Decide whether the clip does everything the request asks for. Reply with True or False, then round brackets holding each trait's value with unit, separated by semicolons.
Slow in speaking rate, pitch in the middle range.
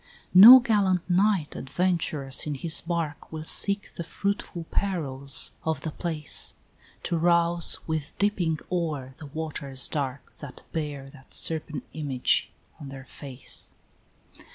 True (130 wpm; 160 Hz)